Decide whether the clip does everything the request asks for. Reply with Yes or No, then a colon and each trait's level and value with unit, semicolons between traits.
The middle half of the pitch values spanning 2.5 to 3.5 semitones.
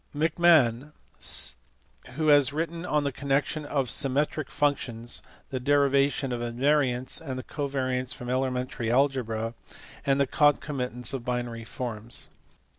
Yes: average, 2.9 semitones